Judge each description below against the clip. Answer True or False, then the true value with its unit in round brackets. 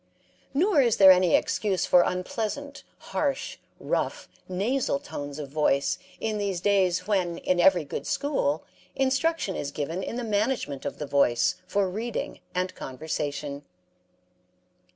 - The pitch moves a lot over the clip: True (7.0 semitones)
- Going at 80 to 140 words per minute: True (135 wpm)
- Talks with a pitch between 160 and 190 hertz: True (185 Hz)